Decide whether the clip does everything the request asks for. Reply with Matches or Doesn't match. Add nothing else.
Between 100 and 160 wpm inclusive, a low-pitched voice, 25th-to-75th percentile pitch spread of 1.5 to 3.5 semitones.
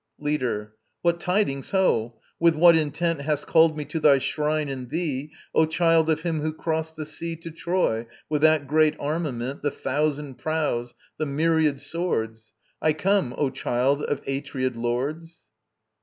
Doesn't match